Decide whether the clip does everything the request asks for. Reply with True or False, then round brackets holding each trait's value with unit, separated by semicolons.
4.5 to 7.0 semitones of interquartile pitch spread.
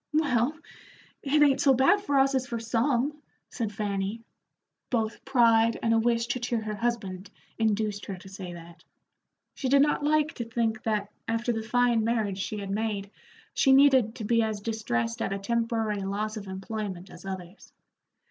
False (3.4 semitones)